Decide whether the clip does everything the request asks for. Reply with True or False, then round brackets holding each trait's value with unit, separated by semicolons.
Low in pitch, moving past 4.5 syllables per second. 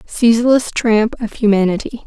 False (225 Hz; 4.9 syllables/s)